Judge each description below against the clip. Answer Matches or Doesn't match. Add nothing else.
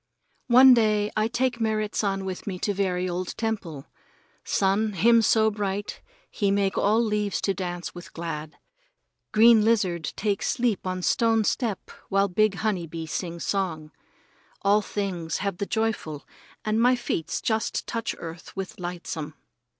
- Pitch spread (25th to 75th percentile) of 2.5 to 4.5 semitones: Matches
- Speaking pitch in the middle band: Doesn't match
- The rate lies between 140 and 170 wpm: Matches